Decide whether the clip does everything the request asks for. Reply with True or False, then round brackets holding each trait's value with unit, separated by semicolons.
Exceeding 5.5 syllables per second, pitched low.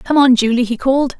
False (6.1 syllables/s; 255 Hz)